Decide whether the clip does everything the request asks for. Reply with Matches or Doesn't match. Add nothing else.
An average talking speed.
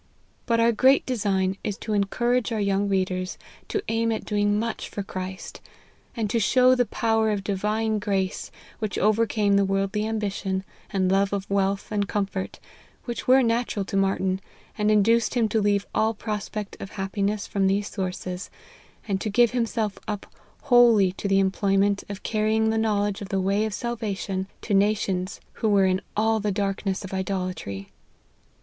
Matches